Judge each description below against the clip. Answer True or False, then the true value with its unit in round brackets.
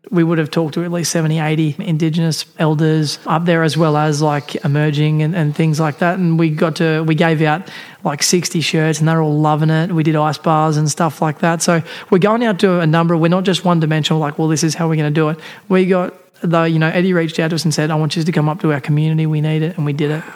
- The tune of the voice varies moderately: False (1.6 semitones)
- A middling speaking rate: False (285 wpm)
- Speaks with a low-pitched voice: False (160 Hz)